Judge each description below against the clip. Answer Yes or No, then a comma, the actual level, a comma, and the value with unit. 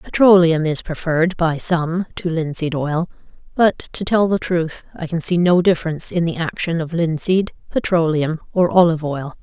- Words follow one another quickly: No, average, 170 wpm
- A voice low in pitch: No, medium, 170 Hz